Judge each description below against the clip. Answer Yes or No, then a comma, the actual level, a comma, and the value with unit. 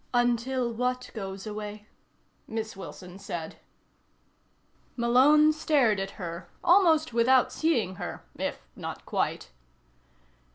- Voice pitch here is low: No, high, 235 Hz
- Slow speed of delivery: Yes, slow, 100 wpm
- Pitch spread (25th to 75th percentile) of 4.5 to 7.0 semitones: Yes, average, 4.8 semitones